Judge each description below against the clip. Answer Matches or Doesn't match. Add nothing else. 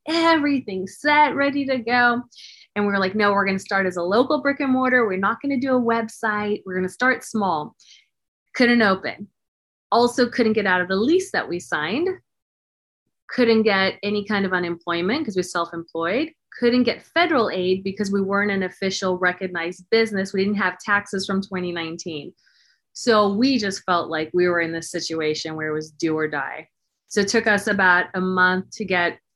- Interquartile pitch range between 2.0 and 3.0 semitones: Doesn't match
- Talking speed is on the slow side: Doesn't match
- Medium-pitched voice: Doesn't match